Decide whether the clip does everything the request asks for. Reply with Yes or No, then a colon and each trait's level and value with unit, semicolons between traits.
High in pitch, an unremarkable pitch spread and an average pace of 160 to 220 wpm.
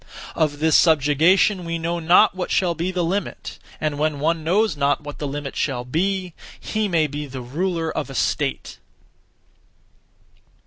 No: medium, 160 Hz; average, 3.5 semitones; average, 165 wpm